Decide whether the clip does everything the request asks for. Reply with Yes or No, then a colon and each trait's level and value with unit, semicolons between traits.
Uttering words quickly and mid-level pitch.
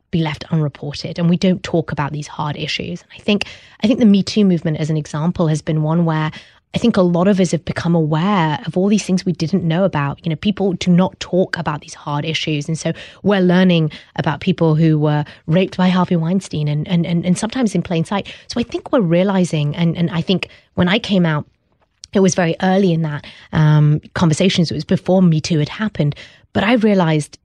Yes: fast, 230 wpm; medium, 170 Hz